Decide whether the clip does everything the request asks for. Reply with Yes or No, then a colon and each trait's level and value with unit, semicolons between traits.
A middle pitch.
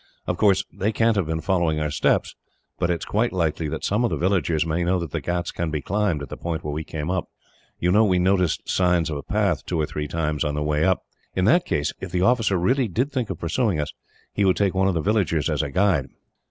No: very low, 90 Hz